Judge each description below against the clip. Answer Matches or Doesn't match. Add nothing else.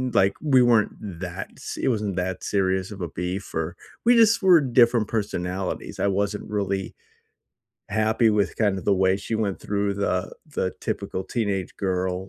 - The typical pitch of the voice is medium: Doesn't match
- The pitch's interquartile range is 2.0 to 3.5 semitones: Matches